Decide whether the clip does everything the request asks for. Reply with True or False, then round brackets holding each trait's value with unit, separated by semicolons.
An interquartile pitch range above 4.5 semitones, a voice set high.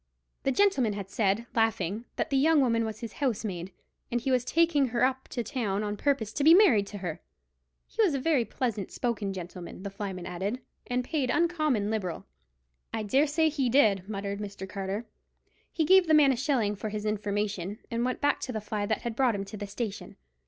True (4.9 semitones; 225 Hz)